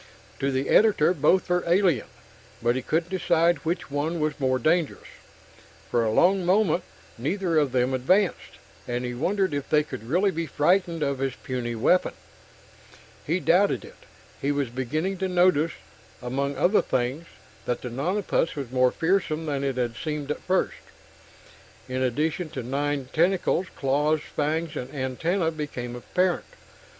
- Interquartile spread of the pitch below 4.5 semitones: No, average, 5.1 semitones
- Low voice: No, medium, 150 Hz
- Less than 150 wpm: No, average, 155 wpm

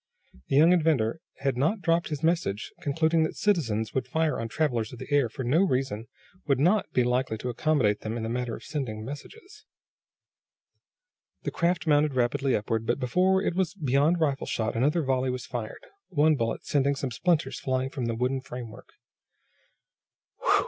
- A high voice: No, low, 135 Hz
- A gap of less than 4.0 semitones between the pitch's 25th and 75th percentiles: No, average, 4.9 semitones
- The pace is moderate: Yes, average, 175 wpm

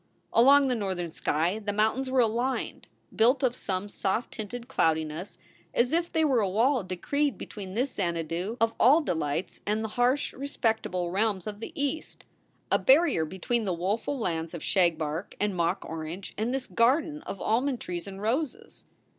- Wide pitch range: Yes, wide, 6.1 semitones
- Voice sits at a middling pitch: No, high, 215 Hz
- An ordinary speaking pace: Yes, average, 170 wpm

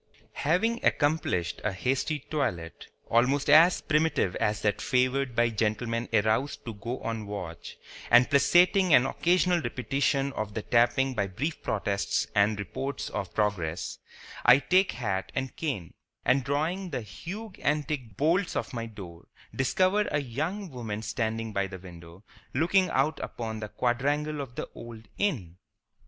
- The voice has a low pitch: Yes, low, 125 Hz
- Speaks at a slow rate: No, average, 145 wpm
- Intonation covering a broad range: Yes, wide, 6.1 semitones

